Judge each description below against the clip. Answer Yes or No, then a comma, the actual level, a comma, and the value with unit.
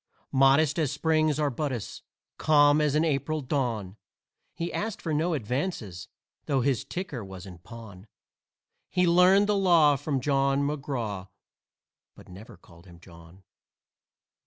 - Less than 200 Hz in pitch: Yes, medium, 140 Hz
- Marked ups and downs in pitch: Yes, wide, 6.5 semitones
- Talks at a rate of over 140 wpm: No, slow, 135 wpm